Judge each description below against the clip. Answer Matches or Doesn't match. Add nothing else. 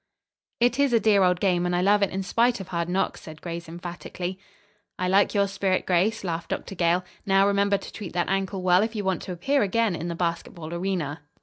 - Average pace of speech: Doesn't match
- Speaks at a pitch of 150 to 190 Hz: Matches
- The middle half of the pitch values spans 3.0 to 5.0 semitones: Doesn't match